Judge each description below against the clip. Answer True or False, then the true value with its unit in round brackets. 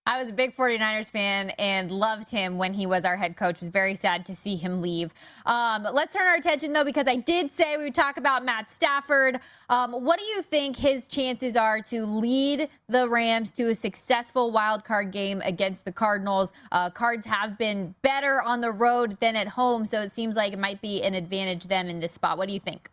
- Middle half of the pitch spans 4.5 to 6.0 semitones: True (4.8 semitones)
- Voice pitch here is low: False (220 Hz)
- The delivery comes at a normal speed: False (230 wpm)